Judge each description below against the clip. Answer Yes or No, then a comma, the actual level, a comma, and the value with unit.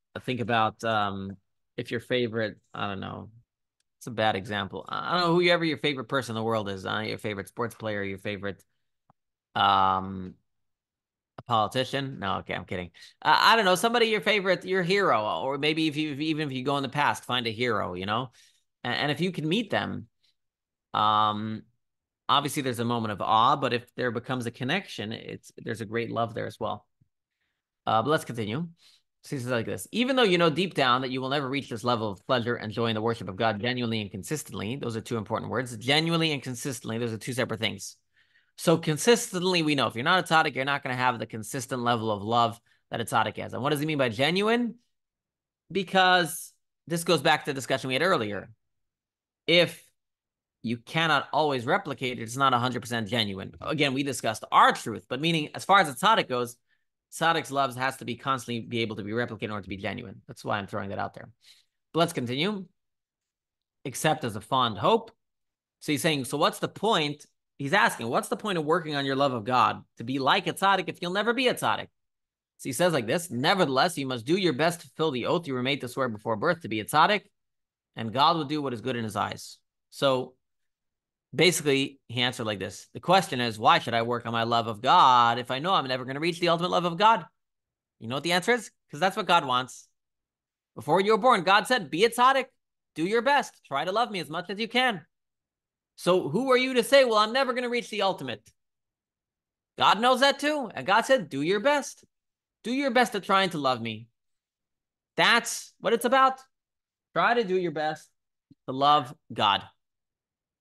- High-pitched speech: No, low, 135 Hz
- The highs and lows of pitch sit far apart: Yes, wide, 7.0 semitones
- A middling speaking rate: No, fast, 215 wpm